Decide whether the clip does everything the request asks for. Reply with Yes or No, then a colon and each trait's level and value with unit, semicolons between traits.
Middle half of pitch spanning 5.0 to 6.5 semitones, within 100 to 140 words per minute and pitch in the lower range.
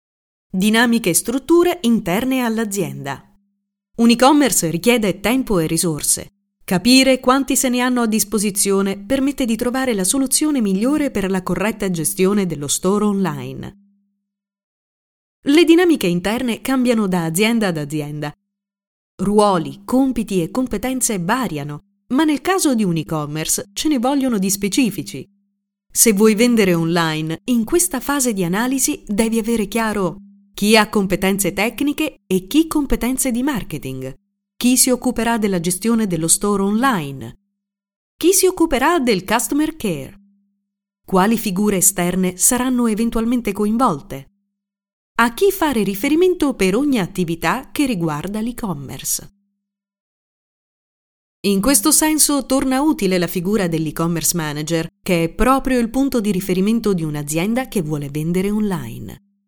No: wide, 5.4 semitones; average, 130 wpm; high, 205 Hz